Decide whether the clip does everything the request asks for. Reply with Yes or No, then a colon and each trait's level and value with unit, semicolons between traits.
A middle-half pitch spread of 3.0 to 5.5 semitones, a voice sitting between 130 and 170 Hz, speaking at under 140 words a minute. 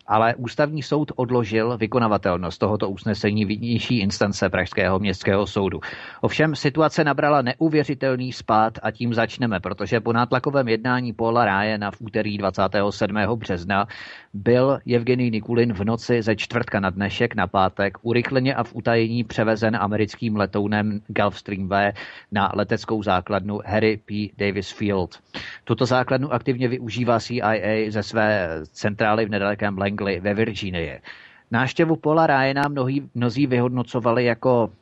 No: average, 3.3 semitones; low, 110 Hz; average, 130 wpm